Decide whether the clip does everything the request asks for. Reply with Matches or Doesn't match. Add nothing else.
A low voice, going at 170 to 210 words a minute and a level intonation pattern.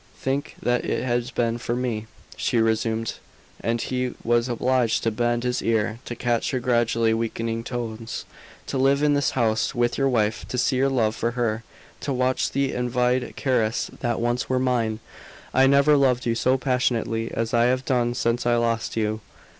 Matches